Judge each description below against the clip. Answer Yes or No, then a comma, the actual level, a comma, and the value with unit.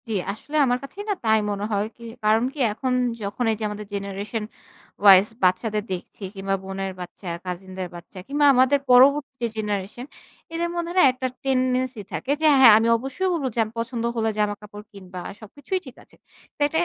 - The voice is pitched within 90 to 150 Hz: No, high, 220 Hz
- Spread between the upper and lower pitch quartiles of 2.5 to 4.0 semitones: No, average, 4.5 semitones